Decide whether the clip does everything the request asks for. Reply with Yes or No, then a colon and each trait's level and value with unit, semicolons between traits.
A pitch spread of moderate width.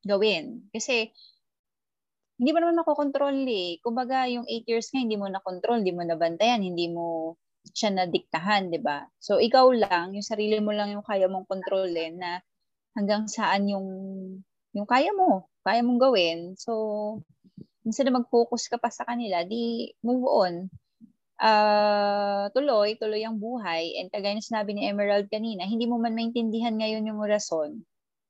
Yes: average, 3.6 semitones